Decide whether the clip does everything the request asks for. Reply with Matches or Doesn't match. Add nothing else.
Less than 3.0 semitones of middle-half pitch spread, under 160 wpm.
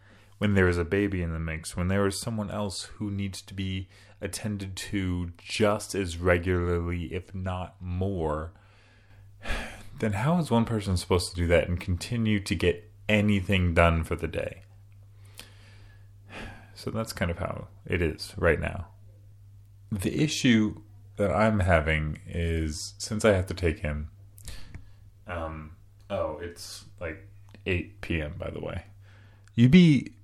Matches